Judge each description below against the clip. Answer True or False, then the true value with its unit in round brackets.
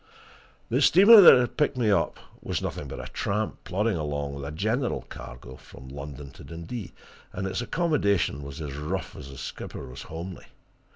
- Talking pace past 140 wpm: True (180 wpm)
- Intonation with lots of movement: True (8.5 semitones)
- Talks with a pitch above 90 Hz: False (85 Hz)